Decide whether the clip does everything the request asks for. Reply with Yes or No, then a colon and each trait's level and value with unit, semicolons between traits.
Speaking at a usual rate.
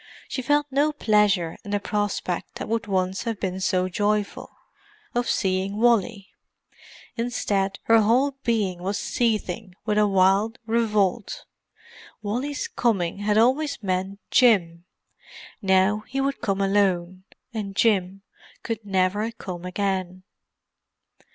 No: slow, 125 wpm